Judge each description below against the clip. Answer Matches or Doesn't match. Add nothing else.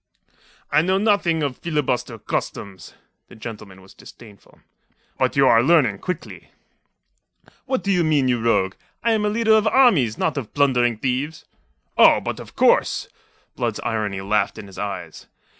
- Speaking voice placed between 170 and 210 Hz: Doesn't match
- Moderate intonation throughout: Doesn't match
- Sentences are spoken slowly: Doesn't match